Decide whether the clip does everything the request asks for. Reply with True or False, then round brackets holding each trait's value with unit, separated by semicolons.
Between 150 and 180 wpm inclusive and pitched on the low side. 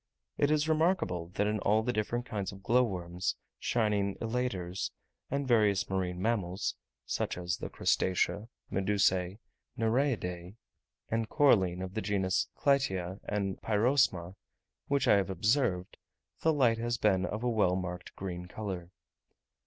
False (135 wpm; 100 Hz)